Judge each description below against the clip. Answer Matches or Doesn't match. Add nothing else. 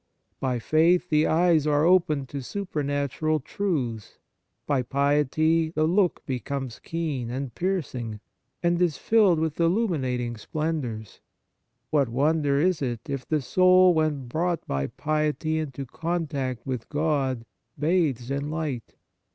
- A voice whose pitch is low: Doesn't match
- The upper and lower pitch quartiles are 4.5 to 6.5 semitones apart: Doesn't match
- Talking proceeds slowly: Matches